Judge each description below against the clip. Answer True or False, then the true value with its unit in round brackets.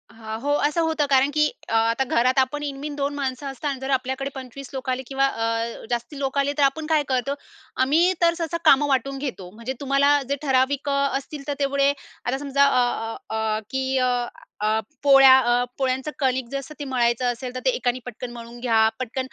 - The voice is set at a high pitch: True (265 Hz)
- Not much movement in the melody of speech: True (2.3 semitones)